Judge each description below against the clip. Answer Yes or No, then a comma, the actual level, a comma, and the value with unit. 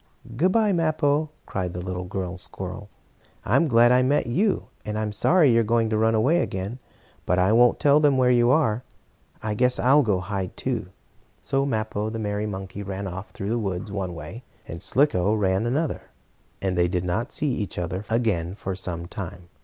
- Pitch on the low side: Yes, low, 110 Hz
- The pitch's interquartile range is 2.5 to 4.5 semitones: No, average, 5.1 semitones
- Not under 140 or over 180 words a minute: No, average, 200 wpm